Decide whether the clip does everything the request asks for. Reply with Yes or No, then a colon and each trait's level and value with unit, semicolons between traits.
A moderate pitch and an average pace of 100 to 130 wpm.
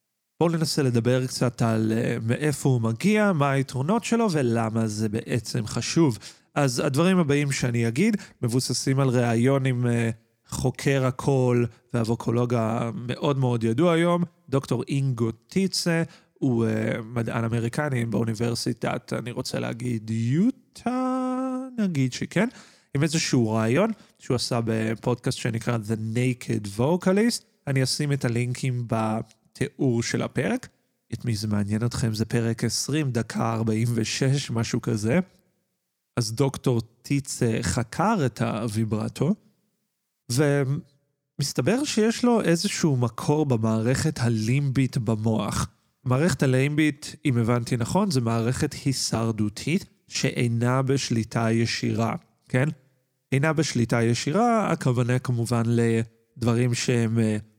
No: low, 125 Hz; average, 110 wpm